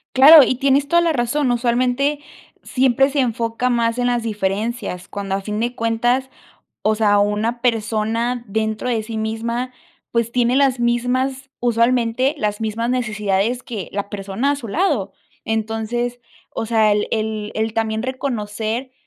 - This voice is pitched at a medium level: No, high, 235 Hz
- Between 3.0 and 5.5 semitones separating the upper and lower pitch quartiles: No, narrow, 2.5 semitones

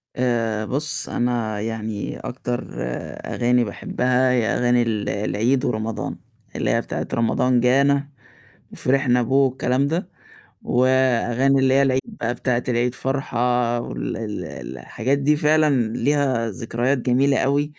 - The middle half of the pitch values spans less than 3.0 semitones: Yes, narrow, 2.6 semitones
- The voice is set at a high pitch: No, low, 125 Hz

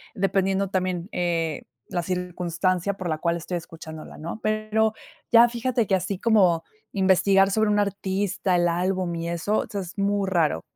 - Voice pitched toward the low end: No, medium, 185 Hz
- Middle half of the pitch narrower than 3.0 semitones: Yes, narrow, 2.6 semitones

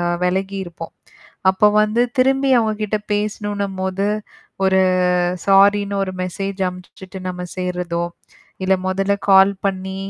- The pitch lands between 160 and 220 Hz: Yes, high, 195 Hz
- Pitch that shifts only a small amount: Yes, narrow, 1.5 semitones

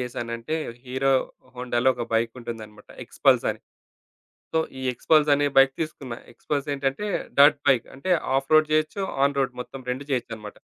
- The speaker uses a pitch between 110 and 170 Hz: Yes, low, 135 Hz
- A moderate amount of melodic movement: Yes, average, 3.3 semitones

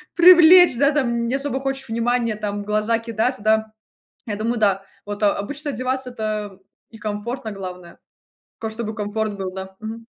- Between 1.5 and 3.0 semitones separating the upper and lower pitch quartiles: No, average, 3.6 semitones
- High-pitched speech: Yes, high, 220 Hz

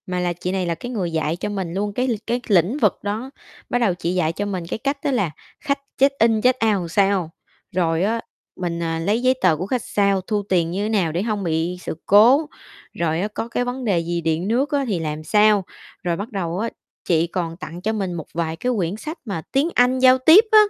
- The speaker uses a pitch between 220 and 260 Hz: No, high, 195 Hz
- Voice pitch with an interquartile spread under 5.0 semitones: No, average, 5.3 semitones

